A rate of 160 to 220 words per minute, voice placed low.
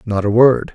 No: fast, 240 wpm; low, 115 Hz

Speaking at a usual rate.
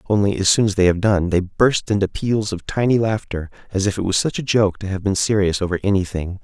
No: fast, 250 wpm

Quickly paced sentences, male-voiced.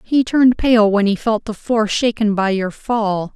No: fast, 215 wpm; female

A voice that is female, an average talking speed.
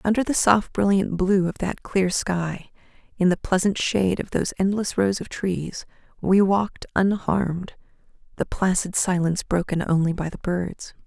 Yes: female; average, 165 wpm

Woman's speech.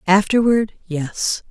Yes: female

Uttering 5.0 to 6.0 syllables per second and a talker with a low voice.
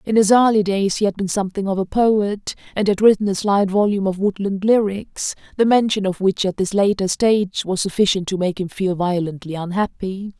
No: 5.4 syllables/s; high, 195 Hz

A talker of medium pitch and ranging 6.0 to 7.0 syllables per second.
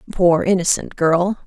No: medium, 180 Hz; 4.2 syllables/s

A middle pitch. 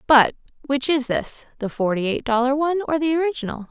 No: very high, 265 Hz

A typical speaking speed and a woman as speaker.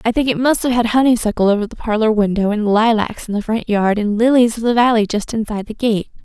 No: fast, 250 wpm; female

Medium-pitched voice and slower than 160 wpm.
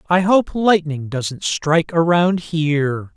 Yes: medium, 165 Hz; slow, 135 wpm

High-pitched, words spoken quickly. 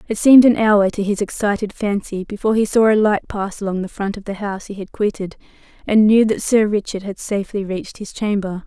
Yes: high, 205 Hz; fast, 230 wpm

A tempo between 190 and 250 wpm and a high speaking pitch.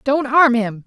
Yes: fast, 205 wpm; very high, 255 Hz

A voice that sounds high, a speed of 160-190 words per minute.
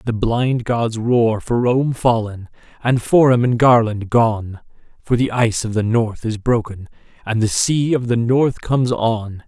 No: low, 115 Hz; average, 175 wpm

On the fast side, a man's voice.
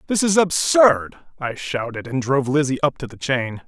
No: average, 195 wpm; male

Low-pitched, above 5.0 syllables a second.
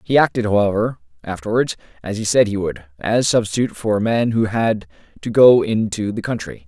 Yes: low, 105 Hz; 5.5 syllables/s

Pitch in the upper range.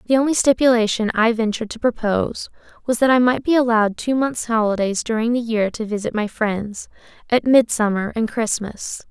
Yes: high, 225 Hz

